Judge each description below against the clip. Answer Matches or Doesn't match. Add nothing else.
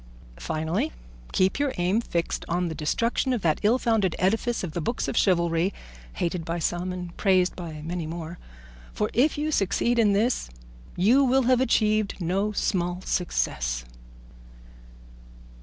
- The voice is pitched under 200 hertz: Matches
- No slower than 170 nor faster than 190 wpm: Doesn't match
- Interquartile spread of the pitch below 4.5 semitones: Doesn't match